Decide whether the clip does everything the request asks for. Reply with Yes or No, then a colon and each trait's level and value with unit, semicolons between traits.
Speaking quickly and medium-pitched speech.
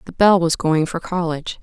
Yes: fast, 220 wpm; medium, 170 Hz